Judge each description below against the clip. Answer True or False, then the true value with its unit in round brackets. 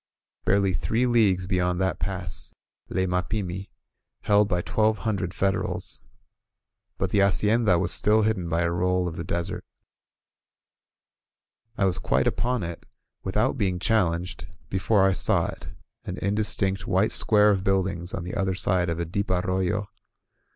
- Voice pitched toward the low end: True (95 Hz)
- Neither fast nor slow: True (150 wpm)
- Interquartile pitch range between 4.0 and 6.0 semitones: False (2.5 semitones)